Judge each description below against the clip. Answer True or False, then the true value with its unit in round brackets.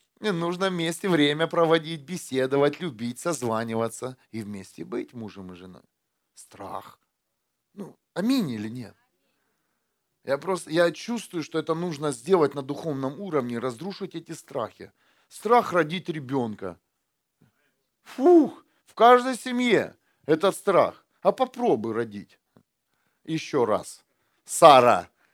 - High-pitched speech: False (160 Hz)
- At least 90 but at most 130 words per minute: True (115 wpm)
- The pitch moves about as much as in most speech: False (7.3 semitones)